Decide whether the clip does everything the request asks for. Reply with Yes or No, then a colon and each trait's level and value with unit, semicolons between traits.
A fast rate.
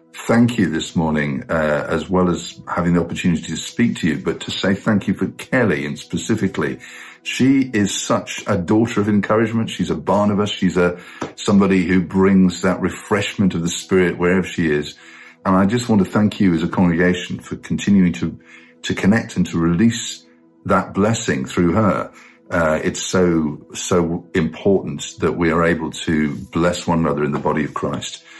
No: average, 185 wpm